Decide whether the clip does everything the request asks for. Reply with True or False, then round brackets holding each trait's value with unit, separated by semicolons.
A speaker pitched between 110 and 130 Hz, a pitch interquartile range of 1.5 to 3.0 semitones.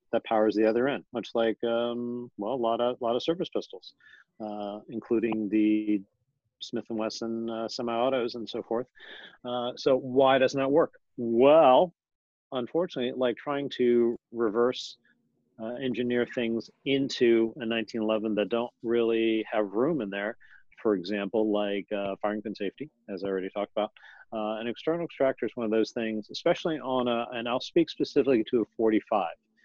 True (115 Hz; 2.4 semitones)